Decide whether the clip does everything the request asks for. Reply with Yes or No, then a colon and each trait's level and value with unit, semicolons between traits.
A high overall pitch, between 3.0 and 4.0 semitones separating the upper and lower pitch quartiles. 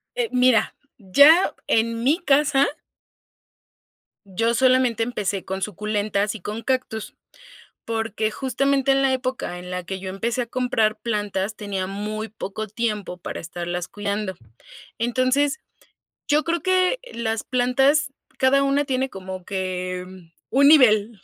No: high, 225 Hz; average, 4.7 semitones